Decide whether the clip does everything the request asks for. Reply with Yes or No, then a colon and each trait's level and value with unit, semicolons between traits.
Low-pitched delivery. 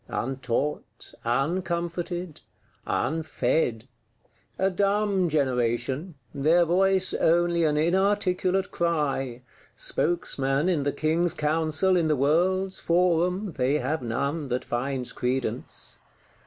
No: medium, 160 Hz